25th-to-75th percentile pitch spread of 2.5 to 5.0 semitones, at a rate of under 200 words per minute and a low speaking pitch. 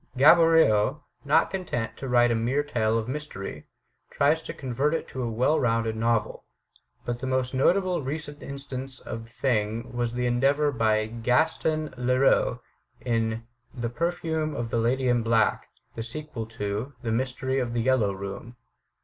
Yes: average, 3.9 semitones; average, 160 wpm; low, 125 Hz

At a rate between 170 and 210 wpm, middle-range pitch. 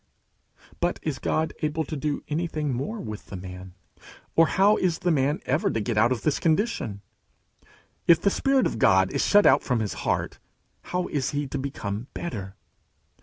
Yes: average, 180 wpm; medium, 145 Hz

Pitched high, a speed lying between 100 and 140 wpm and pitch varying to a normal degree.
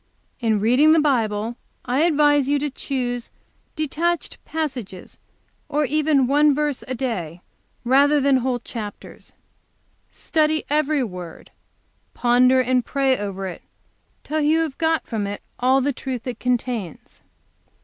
Yes: very high, 260 Hz; slow, 135 wpm; average, 4.0 semitones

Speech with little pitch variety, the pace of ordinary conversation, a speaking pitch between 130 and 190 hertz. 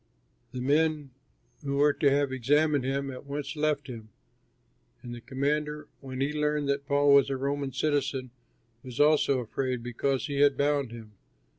Yes: narrow, 2.0 semitones; average, 165 wpm; medium, 140 Hz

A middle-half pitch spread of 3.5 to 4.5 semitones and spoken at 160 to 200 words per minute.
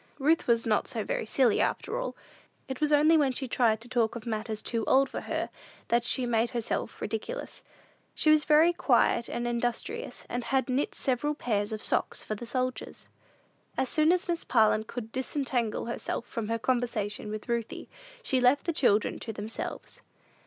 Yes: average, 3.8 semitones; average, 180 wpm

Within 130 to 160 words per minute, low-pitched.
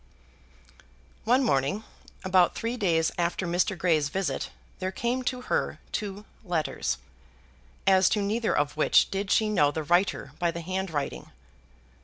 No: average, 140 wpm; medium, 185 Hz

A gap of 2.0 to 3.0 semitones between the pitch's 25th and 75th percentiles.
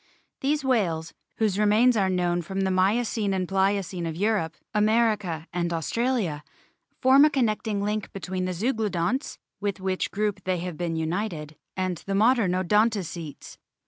No: average, 3.7 semitones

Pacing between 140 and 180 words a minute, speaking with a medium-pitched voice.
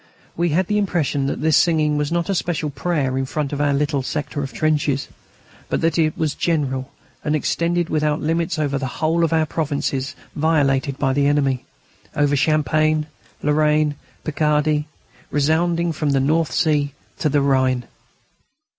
Yes: average, 165 wpm; medium, 150 Hz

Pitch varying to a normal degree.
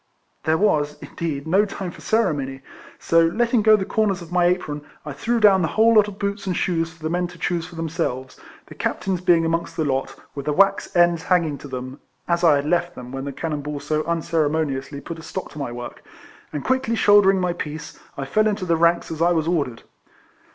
Yes: average, 4.1 semitones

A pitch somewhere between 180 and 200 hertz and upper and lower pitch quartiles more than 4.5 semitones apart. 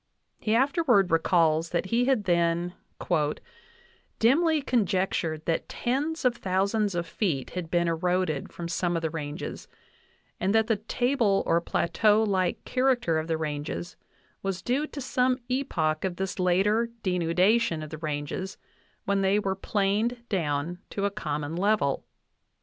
Yes: high, 190 Hz; average, 5.0 semitones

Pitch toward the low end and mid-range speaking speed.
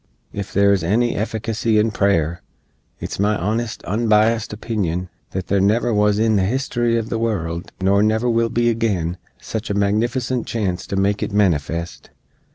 Yes: low, 105 Hz; average, 165 wpm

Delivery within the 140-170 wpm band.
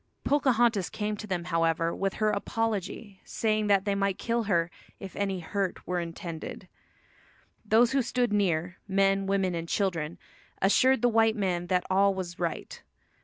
Yes: average, 160 wpm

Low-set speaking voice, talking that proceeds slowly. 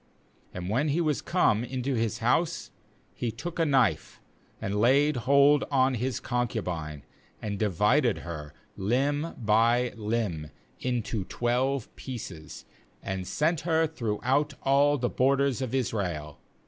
Yes: low, 125 Hz; slow, 130 wpm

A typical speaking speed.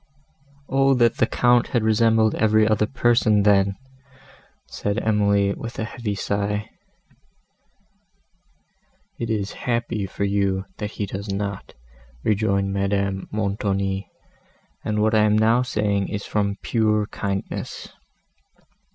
No: slow, 120 wpm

